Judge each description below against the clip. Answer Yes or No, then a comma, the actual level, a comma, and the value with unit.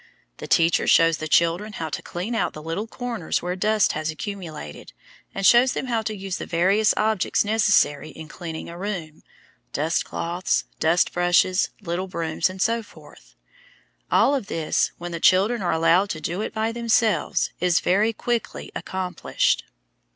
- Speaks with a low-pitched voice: No, medium, 185 Hz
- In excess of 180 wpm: No, average, 160 wpm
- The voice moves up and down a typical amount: Yes, average, 4.4 semitones